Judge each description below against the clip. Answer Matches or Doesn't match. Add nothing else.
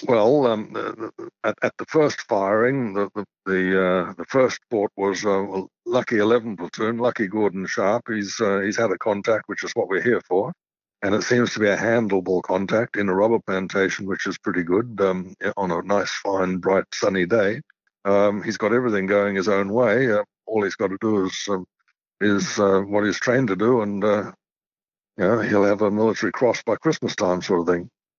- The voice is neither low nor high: Doesn't match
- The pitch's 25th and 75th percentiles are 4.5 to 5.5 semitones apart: Doesn't match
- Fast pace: Matches